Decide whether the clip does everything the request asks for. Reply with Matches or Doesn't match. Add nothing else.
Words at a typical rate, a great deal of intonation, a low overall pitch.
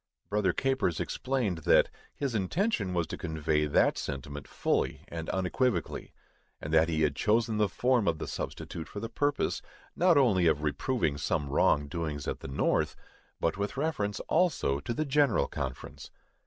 Matches